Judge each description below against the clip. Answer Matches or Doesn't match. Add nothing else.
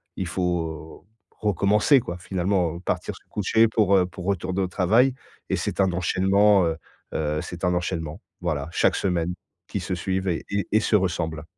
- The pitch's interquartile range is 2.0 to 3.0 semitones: Matches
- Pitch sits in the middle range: Doesn't match